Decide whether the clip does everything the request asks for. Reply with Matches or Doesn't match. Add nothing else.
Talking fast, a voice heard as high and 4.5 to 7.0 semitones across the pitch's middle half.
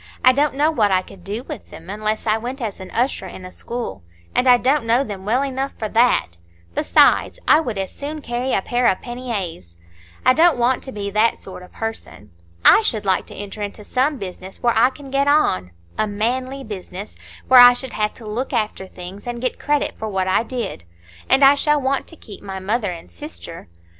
Matches